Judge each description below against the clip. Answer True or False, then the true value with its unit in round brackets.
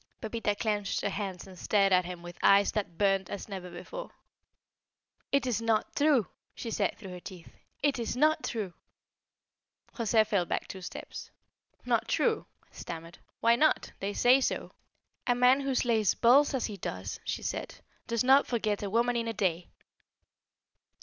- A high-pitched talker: True (215 Hz)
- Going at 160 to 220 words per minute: True (170 wpm)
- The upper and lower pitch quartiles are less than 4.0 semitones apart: False (4.3 semitones)